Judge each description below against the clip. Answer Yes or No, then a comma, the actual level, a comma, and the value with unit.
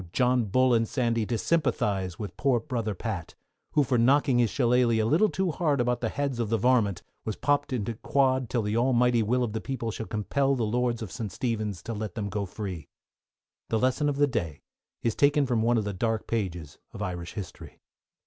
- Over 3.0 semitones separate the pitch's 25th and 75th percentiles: Yes, average, 3.5 semitones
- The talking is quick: Yes, fast, 210 wpm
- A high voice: No, low, 115 Hz